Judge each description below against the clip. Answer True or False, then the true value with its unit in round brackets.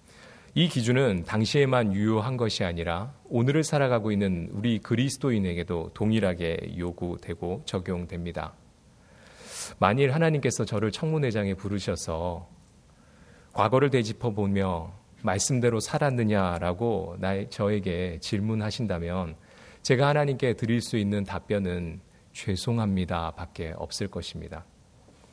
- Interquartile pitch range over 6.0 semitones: False (5.2 semitones)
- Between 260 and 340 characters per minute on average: True (285 characters per minute)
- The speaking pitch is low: True (100 Hz)